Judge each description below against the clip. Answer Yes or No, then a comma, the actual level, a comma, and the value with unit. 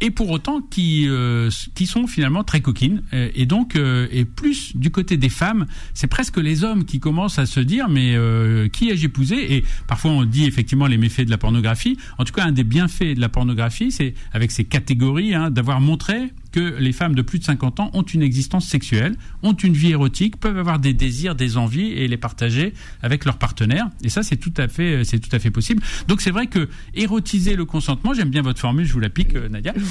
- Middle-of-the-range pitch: Yes, medium, 145 Hz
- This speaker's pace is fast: Yes, fast, 230 wpm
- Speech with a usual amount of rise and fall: No, wide, 6.6 semitones